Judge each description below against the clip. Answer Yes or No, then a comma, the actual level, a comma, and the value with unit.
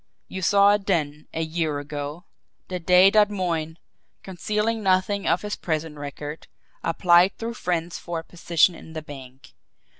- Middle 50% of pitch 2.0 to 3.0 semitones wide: No, average, 3.9 semitones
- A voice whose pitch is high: No, medium, 170 Hz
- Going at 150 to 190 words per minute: Yes, average, 155 wpm